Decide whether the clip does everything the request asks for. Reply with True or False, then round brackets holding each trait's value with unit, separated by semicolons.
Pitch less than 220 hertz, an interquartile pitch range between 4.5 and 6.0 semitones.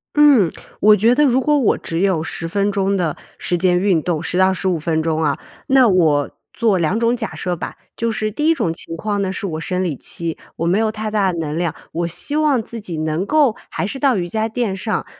True (190 Hz; 5.1 semitones)